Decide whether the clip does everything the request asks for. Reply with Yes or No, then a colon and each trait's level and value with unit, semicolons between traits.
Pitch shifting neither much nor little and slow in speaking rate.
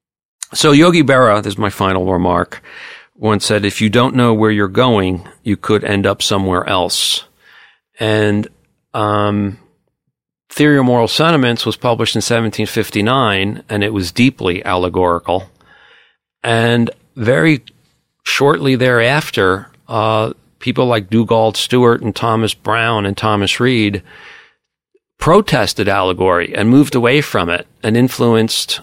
Yes: average, 3.4 semitones; slow, 130 wpm